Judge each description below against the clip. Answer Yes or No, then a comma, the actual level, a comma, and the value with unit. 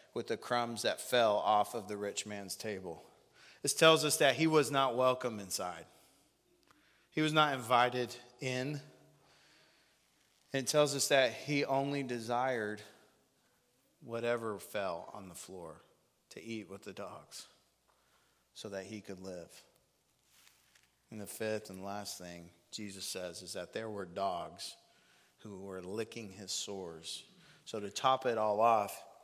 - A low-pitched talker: Yes, low, 115 Hz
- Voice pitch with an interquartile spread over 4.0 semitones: Yes, average, 4.5 semitones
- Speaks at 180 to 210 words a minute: No, average, 145 wpm